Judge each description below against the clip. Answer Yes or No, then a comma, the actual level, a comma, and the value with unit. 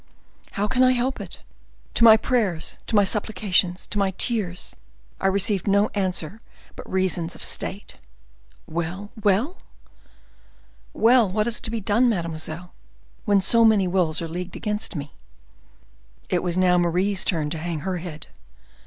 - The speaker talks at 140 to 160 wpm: Yes, average, 155 wpm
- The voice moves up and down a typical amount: Yes, average, 3.6 semitones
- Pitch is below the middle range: No, high, 190 Hz